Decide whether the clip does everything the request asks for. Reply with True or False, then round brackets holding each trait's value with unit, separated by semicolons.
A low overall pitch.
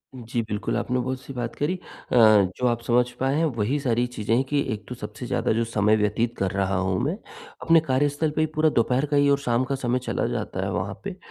True (125 Hz)